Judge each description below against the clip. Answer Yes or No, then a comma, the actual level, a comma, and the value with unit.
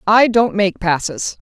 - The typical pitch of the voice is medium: No, high, 200 Hz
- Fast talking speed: No, average, 165 wpm